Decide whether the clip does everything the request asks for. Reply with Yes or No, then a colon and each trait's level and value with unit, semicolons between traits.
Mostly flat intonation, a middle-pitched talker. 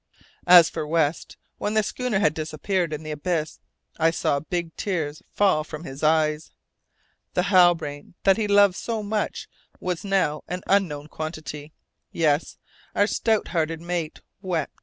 No: average, 3.8 semitones; medium, 165 Hz